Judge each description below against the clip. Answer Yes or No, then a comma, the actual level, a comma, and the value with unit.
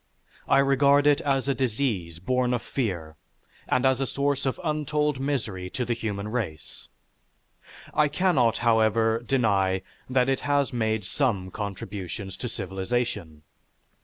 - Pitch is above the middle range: No, low, 120 Hz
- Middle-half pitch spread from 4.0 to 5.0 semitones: No, wide, 5.5 semitones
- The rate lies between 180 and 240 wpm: No, slow, 135 wpm